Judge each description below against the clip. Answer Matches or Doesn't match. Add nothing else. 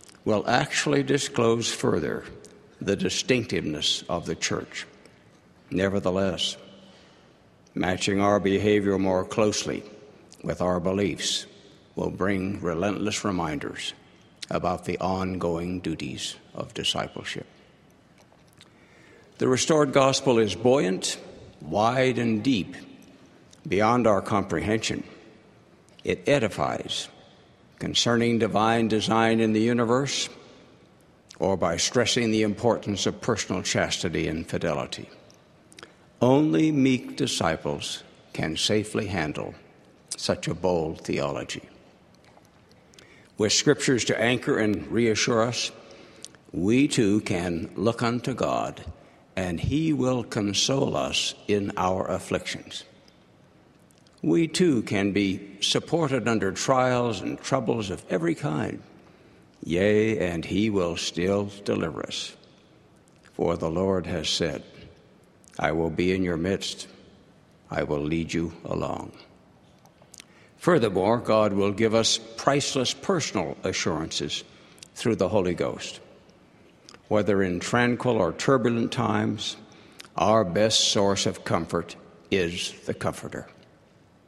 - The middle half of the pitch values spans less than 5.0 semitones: Matches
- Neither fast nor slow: Doesn't match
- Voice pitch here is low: Matches